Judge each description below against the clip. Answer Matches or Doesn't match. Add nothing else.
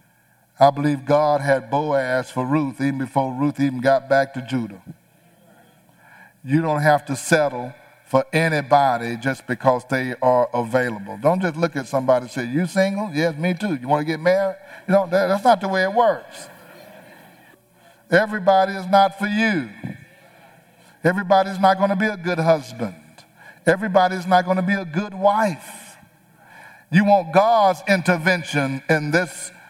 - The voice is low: Doesn't match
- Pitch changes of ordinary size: Doesn't match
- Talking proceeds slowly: Doesn't match